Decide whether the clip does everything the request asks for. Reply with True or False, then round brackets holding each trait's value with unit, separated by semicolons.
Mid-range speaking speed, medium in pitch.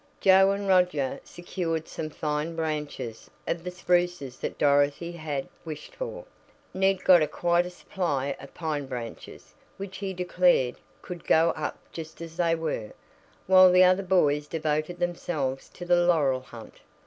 True (150 wpm; 165 Hz)